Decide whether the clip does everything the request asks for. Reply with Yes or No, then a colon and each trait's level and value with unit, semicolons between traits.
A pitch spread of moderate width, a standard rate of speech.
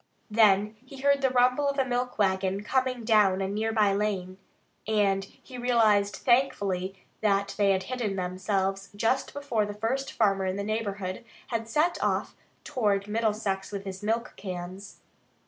Yes: average, 3.6 semitones; average, 160 wpm